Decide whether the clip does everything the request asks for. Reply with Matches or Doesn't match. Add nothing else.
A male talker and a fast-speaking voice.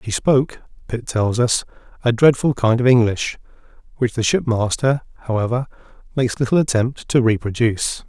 Doesn't match